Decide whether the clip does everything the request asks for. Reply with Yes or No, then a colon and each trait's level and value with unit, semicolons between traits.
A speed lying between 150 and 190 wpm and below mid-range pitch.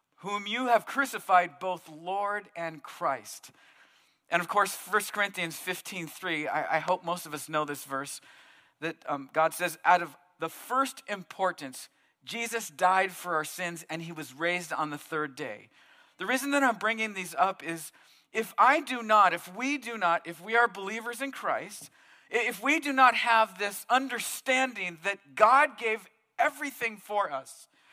No: average, 170 wpm; high, 195 Hz